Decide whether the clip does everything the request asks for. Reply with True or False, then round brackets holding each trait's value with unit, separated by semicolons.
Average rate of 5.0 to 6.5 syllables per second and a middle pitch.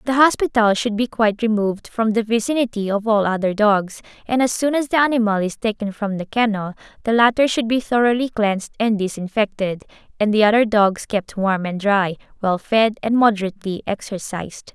False (5.5 syllables/s; 215 Hz)